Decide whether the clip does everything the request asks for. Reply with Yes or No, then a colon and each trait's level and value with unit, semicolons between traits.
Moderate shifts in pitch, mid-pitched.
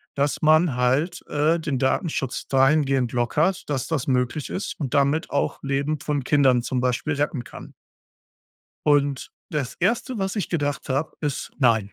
Yes: average, 3.0 semitones; medium, 145 Hz